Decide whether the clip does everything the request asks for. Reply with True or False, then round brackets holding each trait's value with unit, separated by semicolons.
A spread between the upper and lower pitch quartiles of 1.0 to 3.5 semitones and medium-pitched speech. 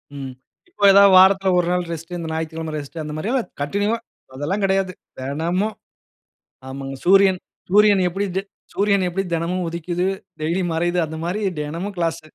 True (3.2 semitones; 175 Hz)